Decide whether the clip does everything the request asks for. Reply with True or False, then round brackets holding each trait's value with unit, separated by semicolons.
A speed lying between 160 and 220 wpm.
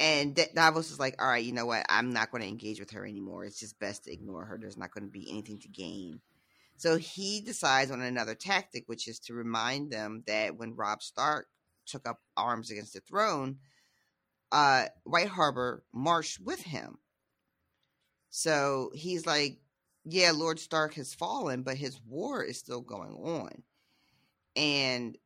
True (175 wpm)